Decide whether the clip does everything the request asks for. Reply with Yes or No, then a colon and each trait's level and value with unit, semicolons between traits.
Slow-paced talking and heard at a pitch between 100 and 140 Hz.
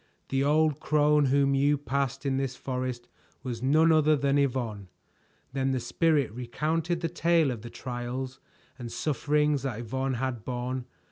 No: average, 155 wpm; low, 135 Hz